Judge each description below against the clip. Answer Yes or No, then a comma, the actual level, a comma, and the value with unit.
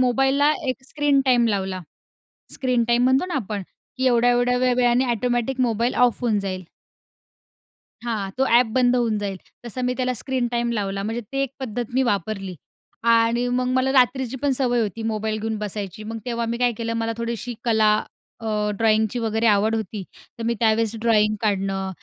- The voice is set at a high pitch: Yes, high, 235 Hz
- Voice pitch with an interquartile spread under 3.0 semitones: Yes, narrow, 2.6 semitones